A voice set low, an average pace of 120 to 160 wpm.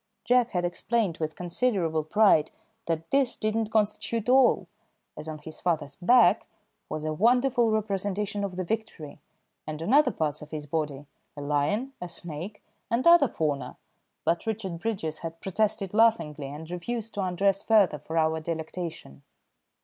No: medium, 180 Hz; average, 155 wpm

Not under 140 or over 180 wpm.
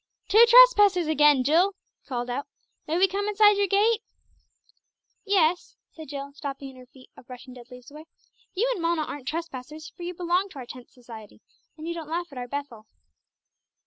No: average, 190 wpm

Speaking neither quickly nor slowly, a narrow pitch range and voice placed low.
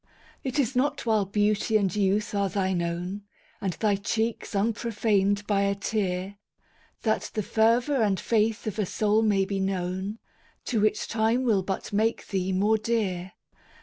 No: average, 160 wpm; narrow, 2.3 semitones; high, 205 Hz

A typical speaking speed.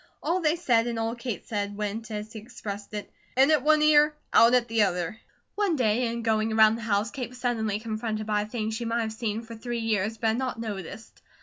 No: fast, 235 wpm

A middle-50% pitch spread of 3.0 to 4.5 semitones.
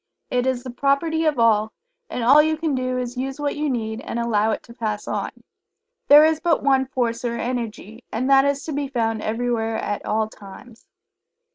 Yes: average, 3.6 semitones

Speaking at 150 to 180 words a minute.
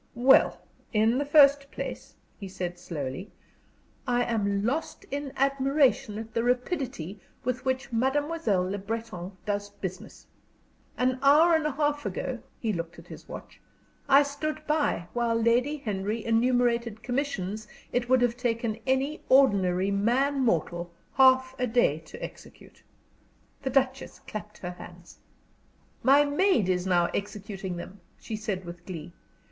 No: average, 140 wpm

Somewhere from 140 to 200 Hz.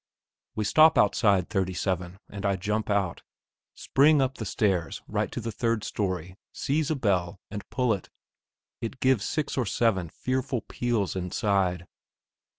No: low, 105 Hz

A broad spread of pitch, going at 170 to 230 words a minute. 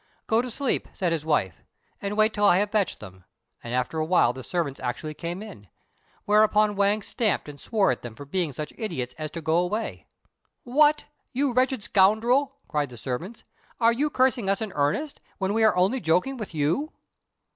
Yes: wide, 6.8 semitones; average, 190 wpm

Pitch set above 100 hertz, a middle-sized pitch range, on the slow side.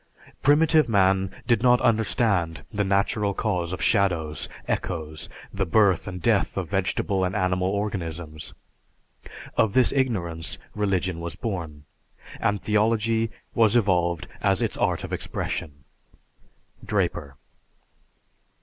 No: very low, 95 Hz; average, 4.3 semitones; slow, 115 wpm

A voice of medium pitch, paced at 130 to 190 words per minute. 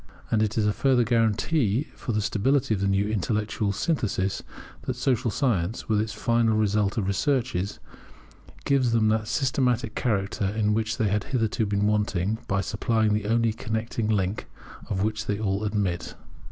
No: low, 110 Hz; average, 175 wpm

